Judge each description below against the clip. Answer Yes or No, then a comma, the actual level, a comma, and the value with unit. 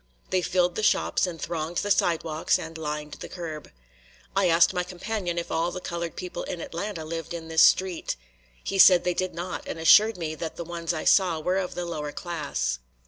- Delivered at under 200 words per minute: No, fast, 205 wpm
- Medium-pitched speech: Yes, medium, 170 Hz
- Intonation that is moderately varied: No, narrow, 1.9 semitones